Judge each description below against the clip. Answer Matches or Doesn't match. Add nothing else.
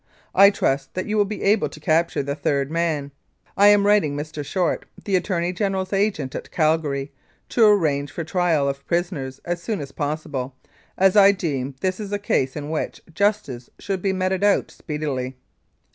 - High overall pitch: Doesn't match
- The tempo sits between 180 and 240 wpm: Matches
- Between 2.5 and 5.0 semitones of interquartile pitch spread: Doesn't match